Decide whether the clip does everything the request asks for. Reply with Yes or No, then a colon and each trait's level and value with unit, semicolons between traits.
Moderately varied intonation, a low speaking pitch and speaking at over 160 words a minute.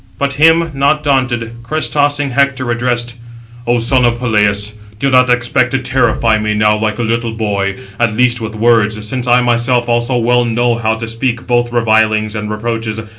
No: narrow, 2.3 semitones; low, 120 Hz; average, 180 wpm